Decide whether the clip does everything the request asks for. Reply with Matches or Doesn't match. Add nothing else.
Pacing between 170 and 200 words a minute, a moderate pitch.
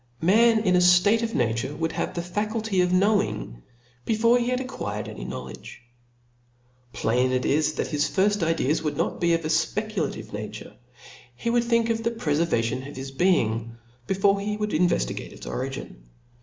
Matches